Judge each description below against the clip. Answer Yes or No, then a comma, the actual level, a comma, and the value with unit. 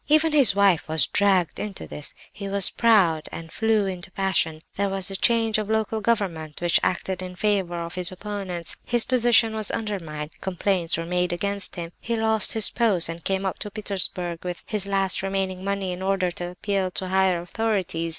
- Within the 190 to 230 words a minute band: Yes, average, 195 wpm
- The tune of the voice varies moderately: Yes, average, 3.0 semitones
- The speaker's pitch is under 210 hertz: Yes, high, 190 Hz